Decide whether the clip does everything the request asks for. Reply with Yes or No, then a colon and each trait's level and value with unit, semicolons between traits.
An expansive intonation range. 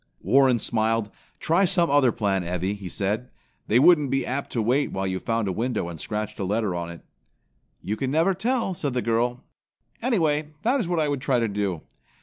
Yes: wide, 6.5 semitones